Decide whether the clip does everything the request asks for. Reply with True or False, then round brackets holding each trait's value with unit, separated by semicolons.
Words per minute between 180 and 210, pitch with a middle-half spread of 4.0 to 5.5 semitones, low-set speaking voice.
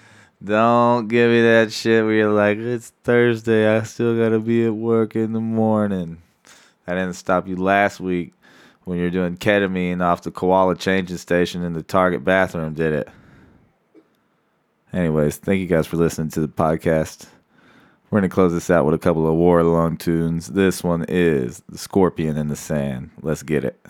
True (185 wpm; 4.7 semitones; 90 Hz)